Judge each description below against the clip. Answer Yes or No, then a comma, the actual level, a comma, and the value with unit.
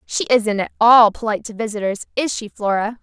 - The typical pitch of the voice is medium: No, high, 220 Hz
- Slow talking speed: No, average, 200 wpm